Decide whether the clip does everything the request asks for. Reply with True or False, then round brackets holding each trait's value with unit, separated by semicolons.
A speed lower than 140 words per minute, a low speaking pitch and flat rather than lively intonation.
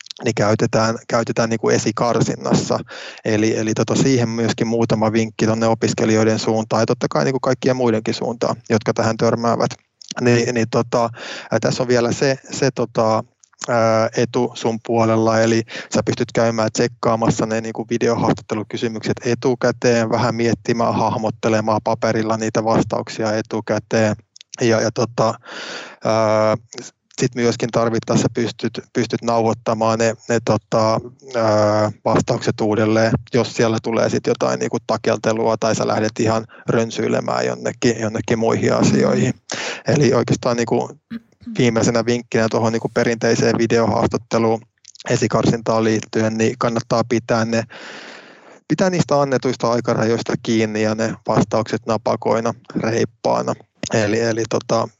True (125 wpm; 115 Hz; 1.2 semitones)